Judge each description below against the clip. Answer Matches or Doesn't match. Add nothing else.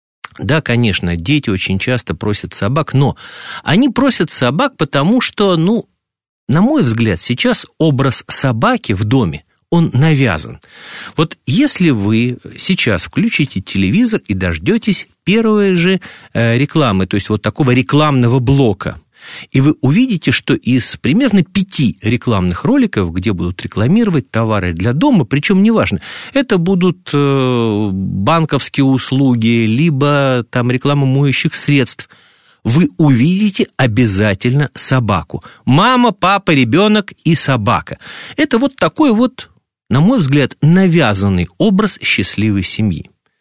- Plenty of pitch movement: Matches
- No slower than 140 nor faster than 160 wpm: Doesn't match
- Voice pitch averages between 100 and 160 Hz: Matches